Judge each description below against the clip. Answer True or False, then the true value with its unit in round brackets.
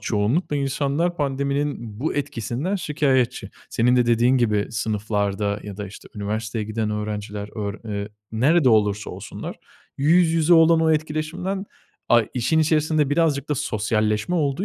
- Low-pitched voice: True (125 Hz)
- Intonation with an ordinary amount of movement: False (6.3 semitones)